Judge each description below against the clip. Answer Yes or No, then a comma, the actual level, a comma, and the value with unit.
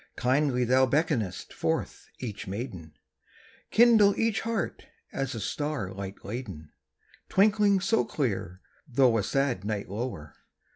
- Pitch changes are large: Yes, wide, 7.5 semitones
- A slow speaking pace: Yes, slow, 125 wpm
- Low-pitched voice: Yes, low, 125 Hz